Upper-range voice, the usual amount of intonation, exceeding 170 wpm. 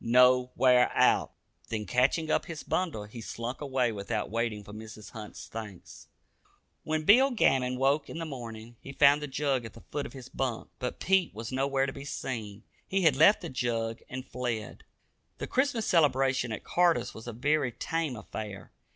No: low, 130 Hz; average, 4.5 semitones; average, 185 wpm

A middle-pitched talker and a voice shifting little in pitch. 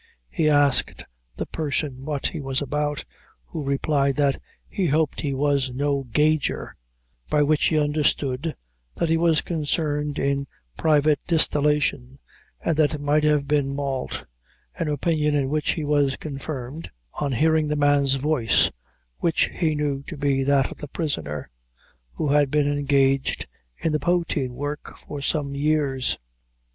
Yes: medium, 145 Hz; narrow, 1.8 semitones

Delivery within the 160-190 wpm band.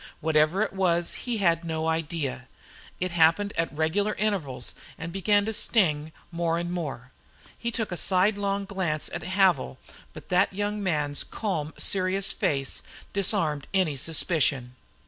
No: average, 145 wpm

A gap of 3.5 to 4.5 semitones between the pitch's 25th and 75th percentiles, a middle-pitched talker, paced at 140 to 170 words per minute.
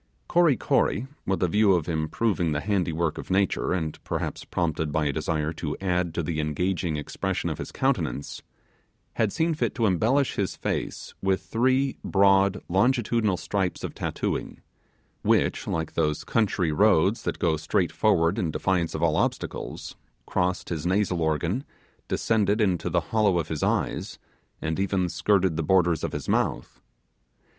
No: average, 4.1 semitones; very low, 90 Hz; average, 160 wpm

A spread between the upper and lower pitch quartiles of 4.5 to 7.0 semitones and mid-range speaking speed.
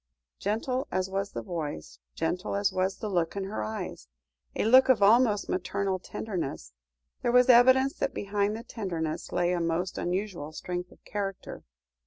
No: average, 3.6 semitones; average, 165 wpm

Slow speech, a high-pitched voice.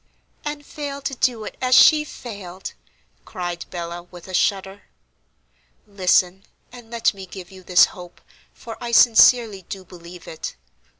No: average, 145 wpm; high, 195 Hz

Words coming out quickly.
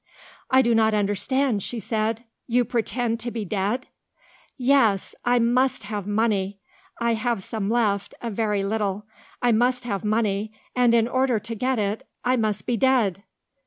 No: average, 160 wpm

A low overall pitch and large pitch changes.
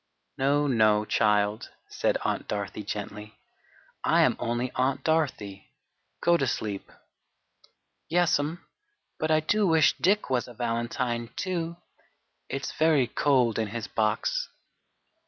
Yes: low, 125 Hz; wide, 6.5 semitones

